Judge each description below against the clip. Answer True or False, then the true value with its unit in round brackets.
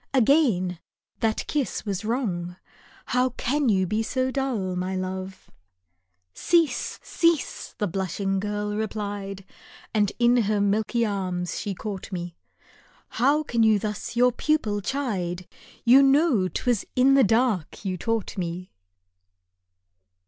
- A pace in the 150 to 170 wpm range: False (135 wpm)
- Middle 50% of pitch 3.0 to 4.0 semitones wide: False (4.9 semitones)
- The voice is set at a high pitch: True (210 Hz)